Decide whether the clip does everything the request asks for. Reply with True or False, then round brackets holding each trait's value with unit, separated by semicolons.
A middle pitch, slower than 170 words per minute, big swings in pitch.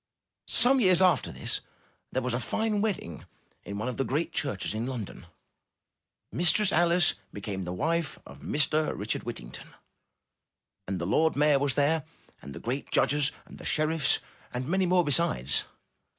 True (145 Hz; 160 wpm; 6.5 semitones)